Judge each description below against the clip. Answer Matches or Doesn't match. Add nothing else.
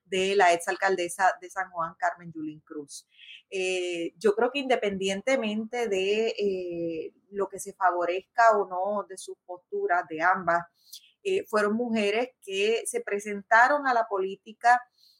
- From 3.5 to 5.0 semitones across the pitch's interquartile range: Matches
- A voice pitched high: Matches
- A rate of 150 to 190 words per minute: Doesn't match